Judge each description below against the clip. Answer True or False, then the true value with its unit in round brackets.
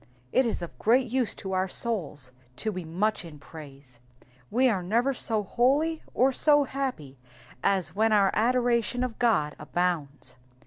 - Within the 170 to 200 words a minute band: False (155 wpm)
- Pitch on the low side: False (215 Hz)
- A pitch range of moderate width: False (7.2 semitones)